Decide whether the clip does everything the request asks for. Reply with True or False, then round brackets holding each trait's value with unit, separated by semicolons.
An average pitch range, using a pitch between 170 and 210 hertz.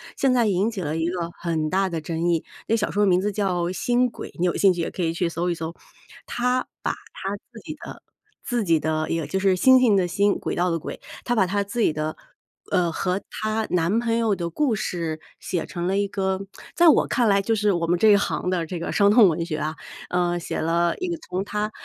True (3.8 semitones; 185 Hz)